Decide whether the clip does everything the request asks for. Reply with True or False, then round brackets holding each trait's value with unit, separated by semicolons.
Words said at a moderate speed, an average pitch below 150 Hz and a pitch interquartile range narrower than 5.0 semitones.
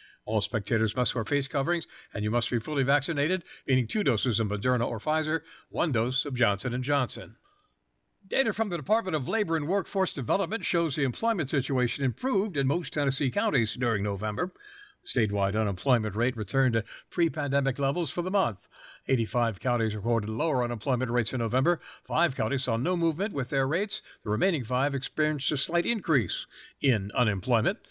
False (170 wpm; 135 Hz; 5.4 semitones)